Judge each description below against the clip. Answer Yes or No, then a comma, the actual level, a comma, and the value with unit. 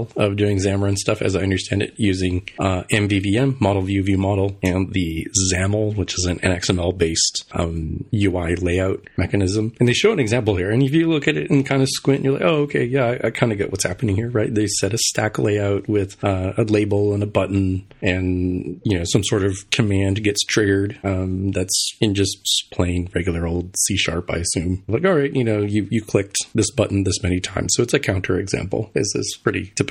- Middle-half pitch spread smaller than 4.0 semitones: Yes, average, 3.1 semitones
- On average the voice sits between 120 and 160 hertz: No, low, 100 Hz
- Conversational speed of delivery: No, fast, 220 wpm